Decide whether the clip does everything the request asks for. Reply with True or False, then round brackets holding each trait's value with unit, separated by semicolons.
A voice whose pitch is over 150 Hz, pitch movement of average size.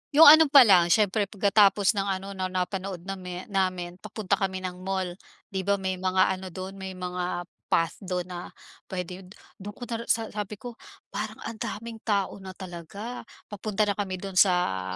False (190 Hz; 2.0 semitones)